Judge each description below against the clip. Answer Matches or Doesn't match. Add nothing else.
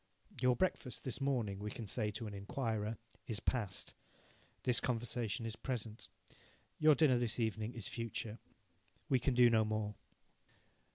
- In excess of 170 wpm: Doesn't match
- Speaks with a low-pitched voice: Matches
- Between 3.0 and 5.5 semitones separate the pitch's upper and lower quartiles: Doesn't match